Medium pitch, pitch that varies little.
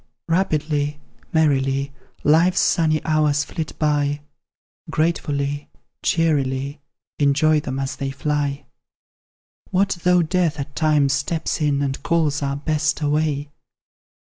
Yes: medium, 150 Hz; narrow, 2.0 semitones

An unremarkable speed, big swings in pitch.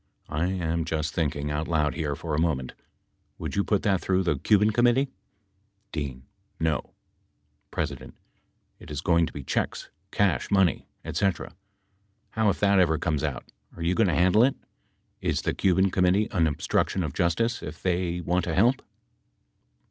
No: average, 170 wpm; average, 4.0 semitones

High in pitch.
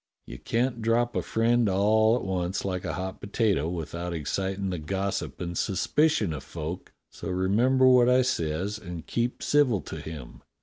No: very low, 95 Hz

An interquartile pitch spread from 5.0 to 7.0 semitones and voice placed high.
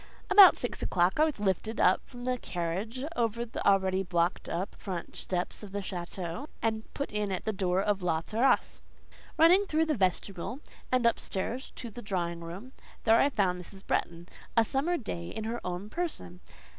Yes: average, 5.3 semitones; high, 205 Hz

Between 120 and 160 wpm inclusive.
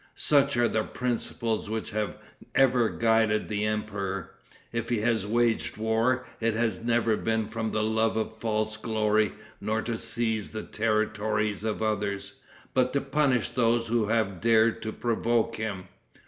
Yes: average, 155 wpm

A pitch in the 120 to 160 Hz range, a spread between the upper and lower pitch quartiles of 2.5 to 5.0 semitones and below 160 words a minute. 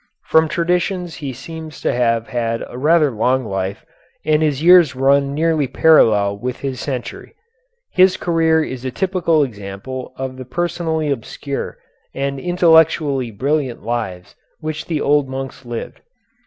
Yes: medium, 140 Hz; average, 4.5 semitones; average, 140 wpm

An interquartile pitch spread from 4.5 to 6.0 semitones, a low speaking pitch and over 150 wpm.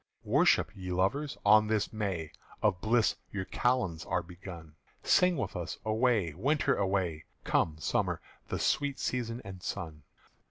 No: average, 5.3 semitones; low, 100 Hz; average, 145 wpm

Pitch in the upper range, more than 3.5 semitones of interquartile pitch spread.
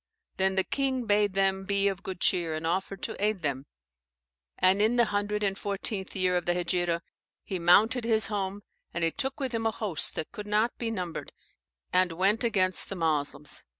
No: high, 195 Hz; average, 3.1 semitones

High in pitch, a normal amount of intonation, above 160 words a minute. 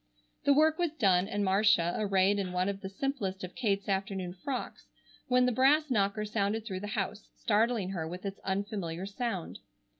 Yes: high, 200 Hz; average, 3.2 semitones; average, 180 wpm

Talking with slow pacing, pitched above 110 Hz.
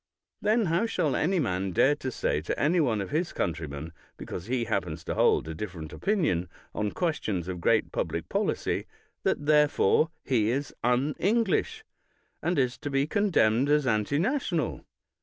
No: average, 160 wpm; low, 135 Hz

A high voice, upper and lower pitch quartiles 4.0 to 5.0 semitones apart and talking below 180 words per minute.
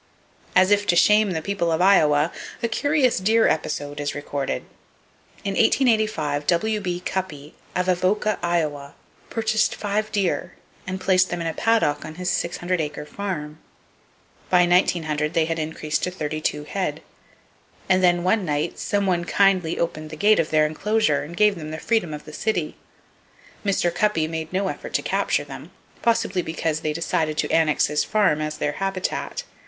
No: medium, 175 Hz; average, 4.5 semitones; average, 170 wpm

